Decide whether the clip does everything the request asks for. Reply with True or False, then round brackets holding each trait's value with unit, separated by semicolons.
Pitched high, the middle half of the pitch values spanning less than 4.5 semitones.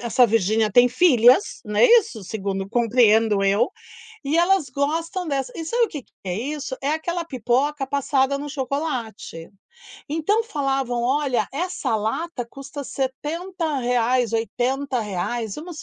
False (265 Hz; 4.9 semitones)